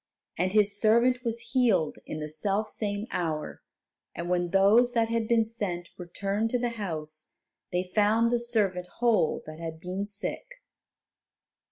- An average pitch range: Yes, average, 4.5 semitones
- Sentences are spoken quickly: No, average, 150 wpm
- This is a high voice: Yes, high, 205 Hz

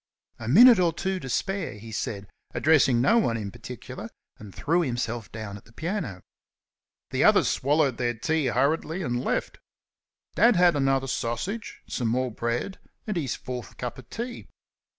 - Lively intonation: Yes, wide, 6.8 semitones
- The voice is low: Yes, low, 130 Hz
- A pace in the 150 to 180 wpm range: Yes, average, 165 wpm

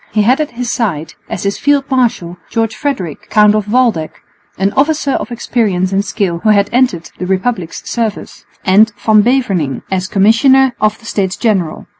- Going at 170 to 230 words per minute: Yes, average, 175 wpm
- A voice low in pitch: No, high, 215 Hz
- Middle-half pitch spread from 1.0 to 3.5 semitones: No, average, 4.5 semitones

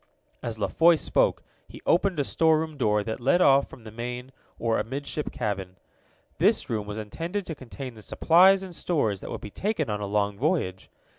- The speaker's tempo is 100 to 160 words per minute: No, average, 195 wpm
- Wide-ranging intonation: Yes, wide, 7.4 semitones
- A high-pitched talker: No, low, 130 Hz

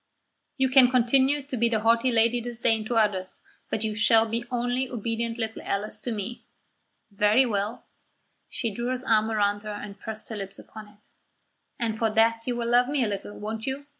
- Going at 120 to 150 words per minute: No, average, 195 wpm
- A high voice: Yes, high, 225 Hz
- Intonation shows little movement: Yes, narrow, 2.3 semitones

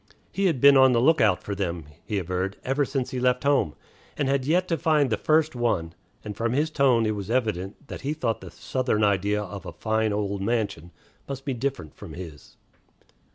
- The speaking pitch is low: Yes, low, 115 Hz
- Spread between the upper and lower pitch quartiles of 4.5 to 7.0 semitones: Yes, wide, 5.5 semitones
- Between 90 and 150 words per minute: No, fast, 205 wpm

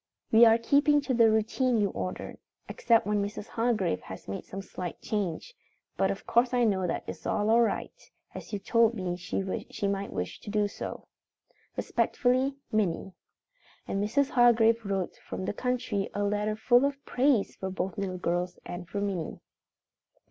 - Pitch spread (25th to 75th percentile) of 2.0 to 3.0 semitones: No, average, 3.7 semitones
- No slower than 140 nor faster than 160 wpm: No, average, 170 wpm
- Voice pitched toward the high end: Yes, high, 210 Hz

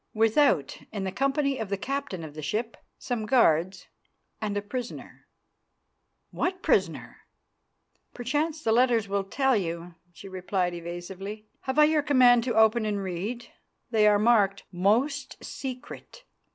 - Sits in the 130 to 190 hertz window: No, high, 220 Hz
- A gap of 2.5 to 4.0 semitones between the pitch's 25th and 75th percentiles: No, average, 5.1 semitones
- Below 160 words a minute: Yes, average, 140 wpm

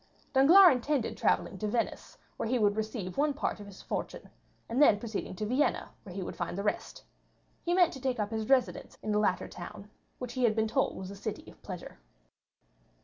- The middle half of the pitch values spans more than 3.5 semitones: Yes, average, 4.4 semitones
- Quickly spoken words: Yes, fast, 210 wpm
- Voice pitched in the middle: No, high, 220 Hz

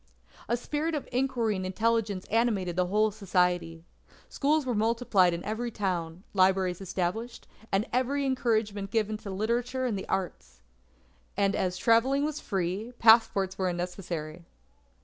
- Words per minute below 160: Yes, average, 140 wpm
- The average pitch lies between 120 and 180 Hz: No, high, 210 Hz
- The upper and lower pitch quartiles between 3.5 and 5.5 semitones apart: Yes, average, 4.2 semitones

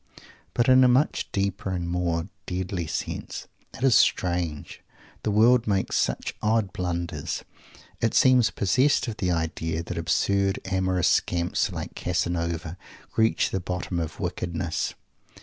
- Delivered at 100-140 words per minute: Yes, slow, 135 wpm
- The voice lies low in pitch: Yes, very low, 95 Hz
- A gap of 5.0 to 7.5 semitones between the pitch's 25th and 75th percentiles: No, average, 4.0 semitones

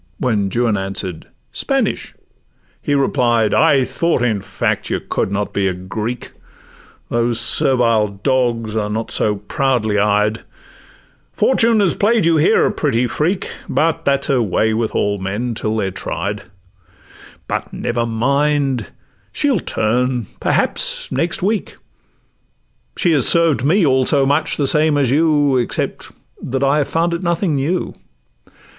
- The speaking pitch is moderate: No, low, 125 Hz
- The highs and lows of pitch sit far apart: Yes, wide, 5.7 semitones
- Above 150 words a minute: No, average, 140 wpm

